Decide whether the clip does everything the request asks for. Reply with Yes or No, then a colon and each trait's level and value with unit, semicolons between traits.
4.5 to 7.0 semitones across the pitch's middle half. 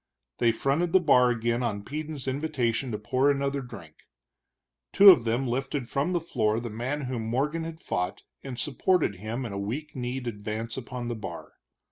No: average, 4.0 semitones